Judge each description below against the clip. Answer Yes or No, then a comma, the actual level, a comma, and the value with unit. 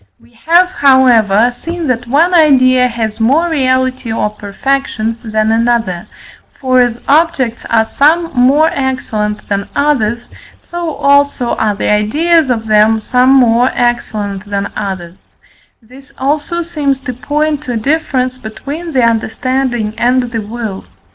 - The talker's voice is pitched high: Yes, very high, 250 Hz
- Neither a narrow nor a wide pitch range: Yes, average, 4.2 semitones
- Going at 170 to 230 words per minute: No, average, 140 wpm